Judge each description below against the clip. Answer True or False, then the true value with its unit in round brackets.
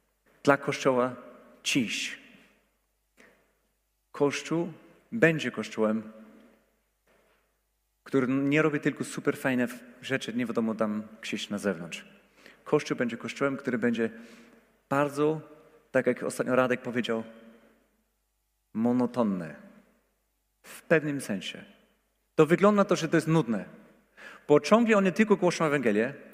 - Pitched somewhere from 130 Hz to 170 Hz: True (140 Hz)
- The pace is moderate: False (105 wpm)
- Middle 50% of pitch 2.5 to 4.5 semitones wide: False (5.1 semitones)